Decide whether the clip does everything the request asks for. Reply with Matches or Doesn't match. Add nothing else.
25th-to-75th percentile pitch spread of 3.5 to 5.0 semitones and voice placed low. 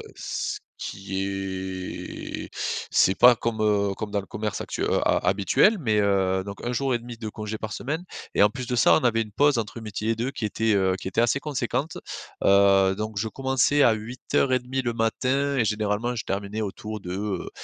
Matches